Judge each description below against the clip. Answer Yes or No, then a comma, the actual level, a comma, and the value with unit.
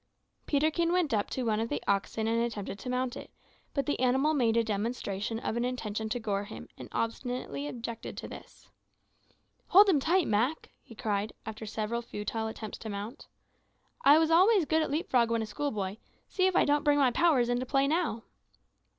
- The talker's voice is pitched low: No, high, 240 Hz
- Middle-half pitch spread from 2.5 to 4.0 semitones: No, average, 5.0 semitones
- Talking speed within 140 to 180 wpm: No, average, 195 wpm